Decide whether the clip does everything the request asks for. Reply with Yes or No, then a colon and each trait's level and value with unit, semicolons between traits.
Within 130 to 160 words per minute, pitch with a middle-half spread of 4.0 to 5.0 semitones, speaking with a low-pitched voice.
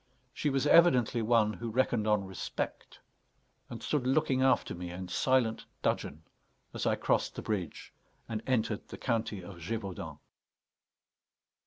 Yes: average, 140 wpm; average, 4.7 semitones; low, 110 Hz